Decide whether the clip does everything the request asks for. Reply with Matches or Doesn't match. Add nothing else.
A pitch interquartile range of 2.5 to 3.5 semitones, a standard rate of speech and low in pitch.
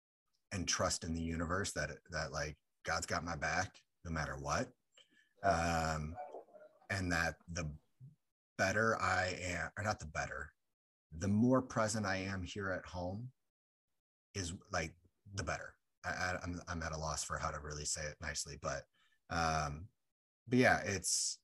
Doesn't match